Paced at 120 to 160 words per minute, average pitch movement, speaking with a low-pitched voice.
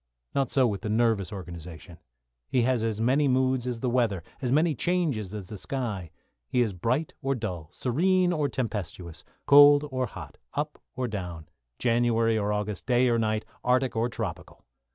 No: average, 175 wpm; average, 4.0 semitones; low, 115 Hz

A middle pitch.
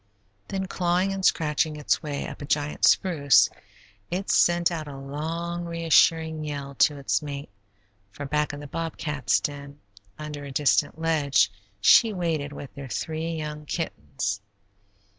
Yes: medium, 150 Hz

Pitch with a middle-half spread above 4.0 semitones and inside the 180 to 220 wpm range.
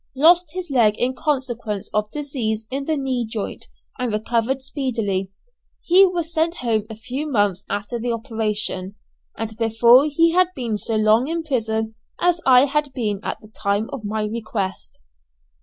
No: average, 4.7 semitones; average, 165 wpm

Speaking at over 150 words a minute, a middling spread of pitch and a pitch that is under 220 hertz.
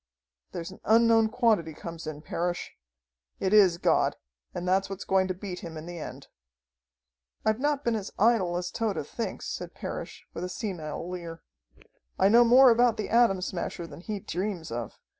Yes: average, 180 wpm; average, 4.5 semitones; high, 190 Hz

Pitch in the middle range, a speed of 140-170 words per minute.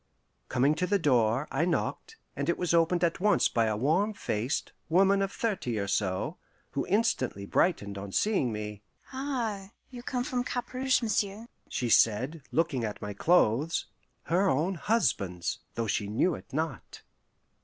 Yes: medium, 165 Hz; average, 165 wpm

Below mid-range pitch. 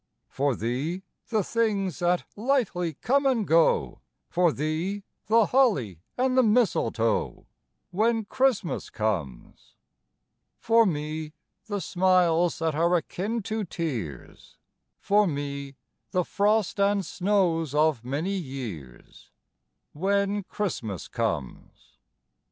No: medium, 175 Hz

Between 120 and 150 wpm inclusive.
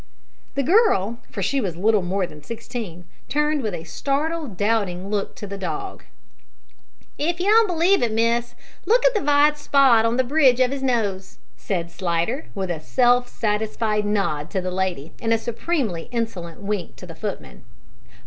No: average, 175 wpm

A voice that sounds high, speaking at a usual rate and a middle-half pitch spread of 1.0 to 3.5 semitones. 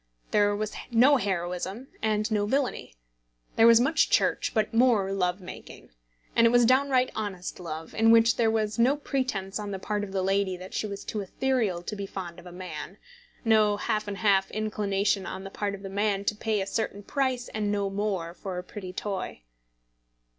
Yes: high, 205 Hz; average, 195 wpm; average, 2.8 semitones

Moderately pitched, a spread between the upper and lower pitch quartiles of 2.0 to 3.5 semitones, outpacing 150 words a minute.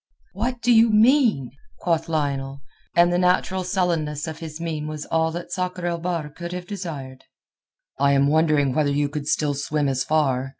No: medium, 160 Hz; average, 3.9 semitones; average, 180 wpm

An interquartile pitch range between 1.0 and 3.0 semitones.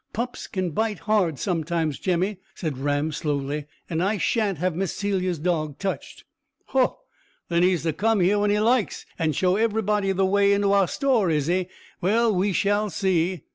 No: average, 3.8 semitones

